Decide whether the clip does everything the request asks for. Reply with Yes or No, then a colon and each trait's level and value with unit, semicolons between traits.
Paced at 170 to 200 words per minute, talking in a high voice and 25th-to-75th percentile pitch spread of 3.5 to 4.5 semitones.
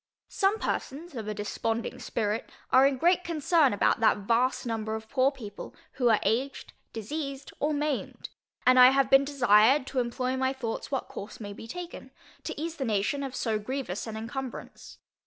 Yes: average, 180 wpm; very high, 255 Hz; average, 3.8 semitones